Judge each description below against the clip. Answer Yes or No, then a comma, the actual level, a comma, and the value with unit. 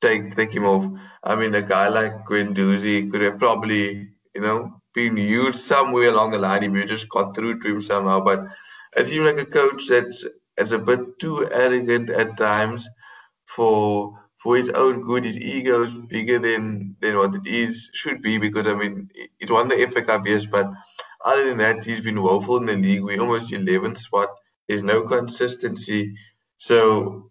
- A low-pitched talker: Yes, low, 110 Hz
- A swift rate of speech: No, average, 190 wpm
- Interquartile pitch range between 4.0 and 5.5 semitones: No, average, 2.7 semitones